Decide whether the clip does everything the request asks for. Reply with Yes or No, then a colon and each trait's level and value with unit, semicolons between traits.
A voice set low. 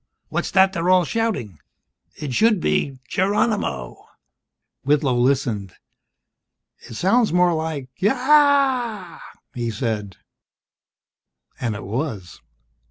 No: medium, 160 Hz